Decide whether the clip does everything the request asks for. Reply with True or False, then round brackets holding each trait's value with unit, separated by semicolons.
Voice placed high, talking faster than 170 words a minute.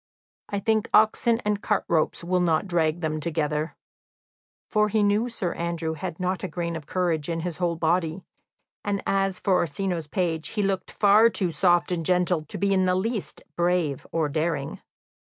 False (180 Hz; 180 wpm)